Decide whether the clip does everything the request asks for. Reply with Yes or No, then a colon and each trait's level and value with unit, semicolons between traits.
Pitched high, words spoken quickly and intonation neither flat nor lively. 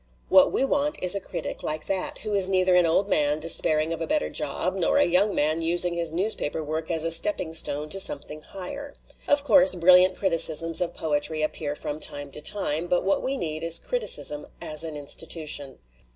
No: medium, 165 Hz; fast, 210 wpm; average, 3.6 semitones